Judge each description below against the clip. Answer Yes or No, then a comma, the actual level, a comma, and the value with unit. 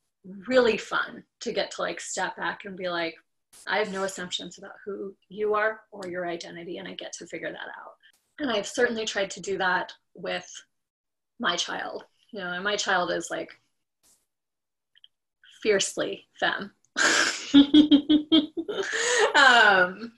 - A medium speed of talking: Yes, average, 145 wpm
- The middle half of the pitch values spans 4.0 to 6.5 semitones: Yes, average, 4.8 semitones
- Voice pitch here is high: Yes, high, 205 Hz